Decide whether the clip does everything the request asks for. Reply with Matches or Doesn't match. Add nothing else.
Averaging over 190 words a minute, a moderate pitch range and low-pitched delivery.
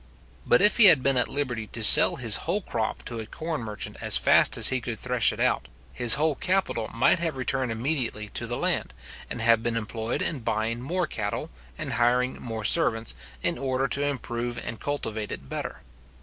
Matches